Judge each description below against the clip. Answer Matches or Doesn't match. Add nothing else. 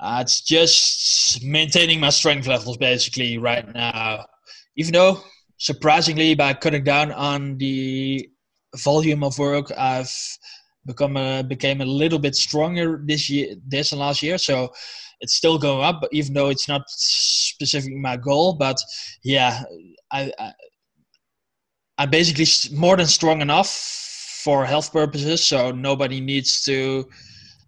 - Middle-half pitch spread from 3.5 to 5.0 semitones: Doesn't match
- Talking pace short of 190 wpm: Matches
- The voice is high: Doesn't match